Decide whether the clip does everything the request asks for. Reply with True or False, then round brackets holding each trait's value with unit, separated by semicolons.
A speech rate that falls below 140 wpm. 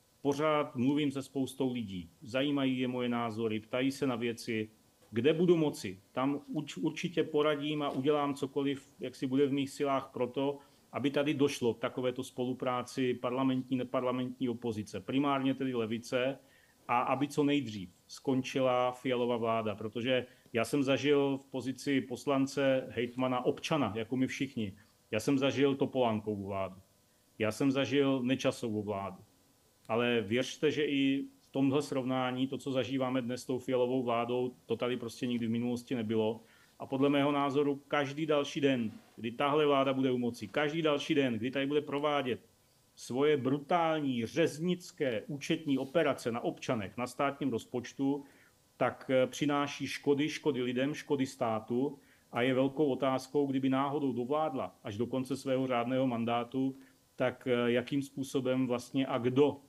False (150 wpm)